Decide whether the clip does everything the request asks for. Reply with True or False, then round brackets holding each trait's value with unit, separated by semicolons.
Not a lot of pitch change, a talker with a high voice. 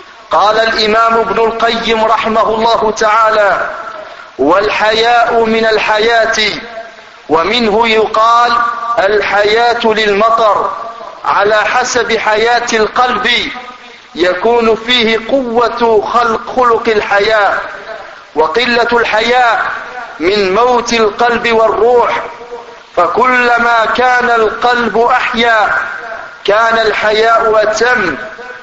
True (1.4 semitones; 225 Hz)